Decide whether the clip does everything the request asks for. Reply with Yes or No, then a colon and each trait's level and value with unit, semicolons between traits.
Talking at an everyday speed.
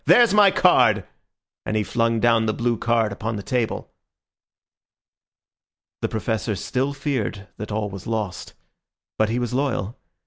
Yes: average, 145 wpm